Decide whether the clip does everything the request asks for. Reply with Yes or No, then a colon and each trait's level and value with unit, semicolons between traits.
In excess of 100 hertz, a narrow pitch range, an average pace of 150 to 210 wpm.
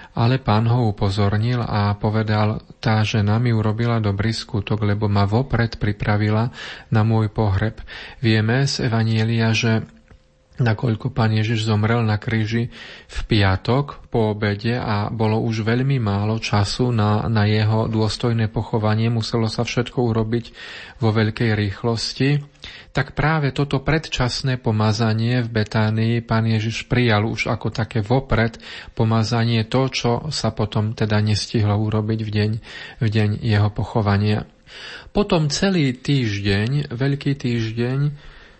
No: low, 115 Hz; narrow, 2.1 semitones; average, 130 wpm